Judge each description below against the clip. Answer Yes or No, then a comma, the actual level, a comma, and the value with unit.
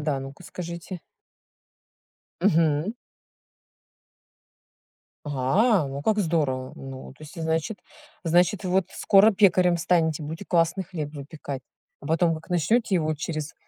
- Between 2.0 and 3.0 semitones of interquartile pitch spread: No, average, 3.6 semitones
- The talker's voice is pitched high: No, medium, 165 Hz